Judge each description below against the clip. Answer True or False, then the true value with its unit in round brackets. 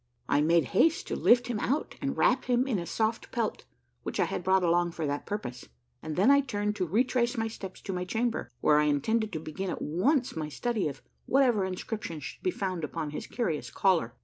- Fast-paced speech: True (215 wpm)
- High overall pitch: True (195 Hz)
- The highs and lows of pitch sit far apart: True (6.6 semitones)